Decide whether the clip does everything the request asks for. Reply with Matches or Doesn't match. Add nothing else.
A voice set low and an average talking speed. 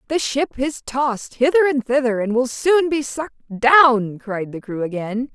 Doesn't match